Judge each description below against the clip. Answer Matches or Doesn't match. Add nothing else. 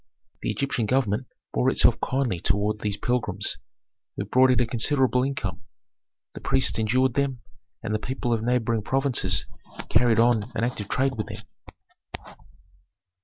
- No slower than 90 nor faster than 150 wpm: Matches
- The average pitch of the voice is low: Matches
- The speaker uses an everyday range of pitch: Matches